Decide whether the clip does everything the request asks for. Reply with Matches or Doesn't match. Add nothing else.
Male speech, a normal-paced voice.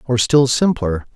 Matches